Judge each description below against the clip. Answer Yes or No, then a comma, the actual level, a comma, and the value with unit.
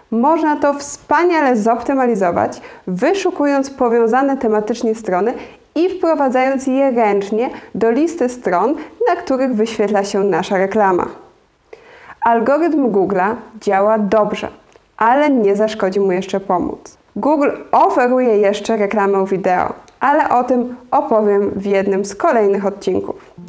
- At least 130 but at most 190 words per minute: No, average, 115 wpm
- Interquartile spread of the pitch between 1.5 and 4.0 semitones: No, average, 5.3 semitones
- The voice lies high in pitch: Yes, high, 230 Hz